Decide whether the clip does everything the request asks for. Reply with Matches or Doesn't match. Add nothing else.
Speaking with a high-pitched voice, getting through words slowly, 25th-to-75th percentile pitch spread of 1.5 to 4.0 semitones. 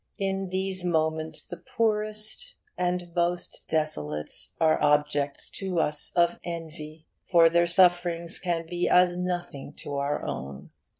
Doesn't match